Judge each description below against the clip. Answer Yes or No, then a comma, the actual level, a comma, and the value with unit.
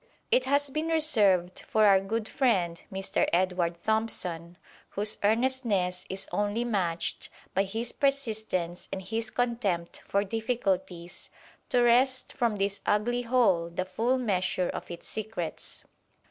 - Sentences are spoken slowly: Yes, slow, 130 wpm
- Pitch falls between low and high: No, high, 210 Hz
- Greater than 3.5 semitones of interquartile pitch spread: Yes, average, 4.7 semitones